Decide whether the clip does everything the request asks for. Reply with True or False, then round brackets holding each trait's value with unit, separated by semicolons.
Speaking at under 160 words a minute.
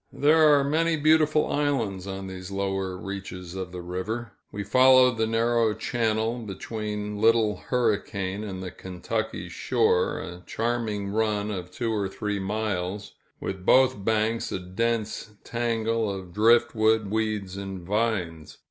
True (140 wpm)